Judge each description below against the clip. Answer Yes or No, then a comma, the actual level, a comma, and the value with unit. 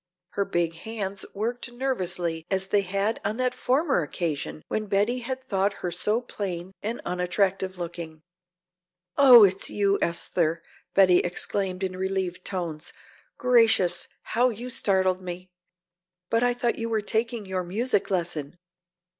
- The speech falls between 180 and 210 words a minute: No, average, 140 wpm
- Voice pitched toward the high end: Yes, high, 195 Hz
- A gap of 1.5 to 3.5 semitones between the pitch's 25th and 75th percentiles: No, average, 4.2 semitones